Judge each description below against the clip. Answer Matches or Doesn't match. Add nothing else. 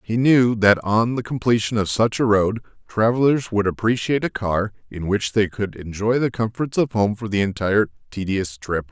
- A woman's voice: Doesn't match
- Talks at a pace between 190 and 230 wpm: Matches